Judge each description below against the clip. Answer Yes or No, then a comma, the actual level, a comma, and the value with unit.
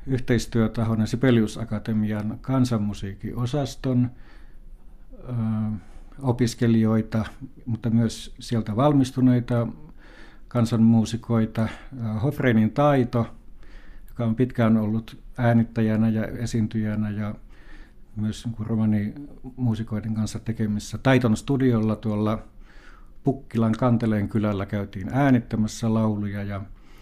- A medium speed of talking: No, slow, 80 wpm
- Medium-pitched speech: No, low, 115 Hz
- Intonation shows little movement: Yes, narrow, 2.2 semitones